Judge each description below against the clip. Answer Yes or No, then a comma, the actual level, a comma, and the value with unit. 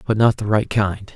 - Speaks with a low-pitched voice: Yes, low, 105 Hz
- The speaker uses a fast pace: Yes, fast, 260 wpm